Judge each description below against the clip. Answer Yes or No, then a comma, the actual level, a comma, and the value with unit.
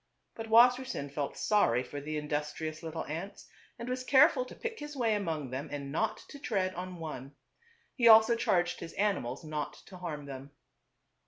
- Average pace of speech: Yes, average, 175 wpm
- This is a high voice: No, medium, 175 Hz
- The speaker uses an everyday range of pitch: No, wide, 7.4 semitones